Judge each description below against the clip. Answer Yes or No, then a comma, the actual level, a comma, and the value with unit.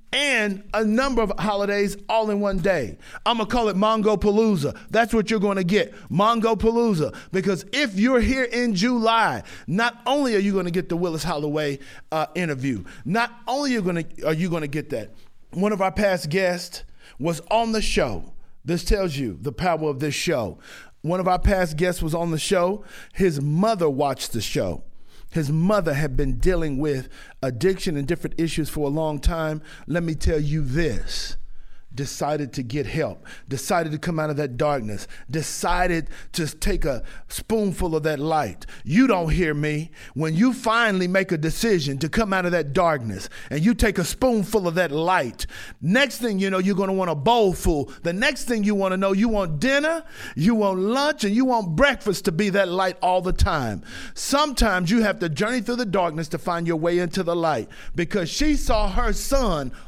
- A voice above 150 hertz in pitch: Yes, medium, 185 Hz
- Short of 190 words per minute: No, average, 200 wpm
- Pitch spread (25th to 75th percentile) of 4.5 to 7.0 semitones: Yes, wide, 5.6 semitones